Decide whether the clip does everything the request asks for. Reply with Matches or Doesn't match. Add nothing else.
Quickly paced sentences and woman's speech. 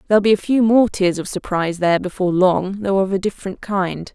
Matches